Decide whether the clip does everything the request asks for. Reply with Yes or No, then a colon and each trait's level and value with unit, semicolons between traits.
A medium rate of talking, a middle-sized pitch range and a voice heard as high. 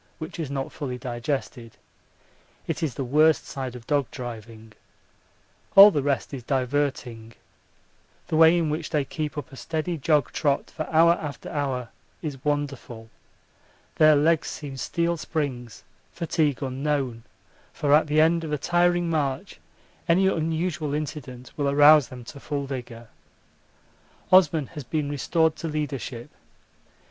No: average, 145 wpm; average, 3.4 semitones; medium, 145 Hz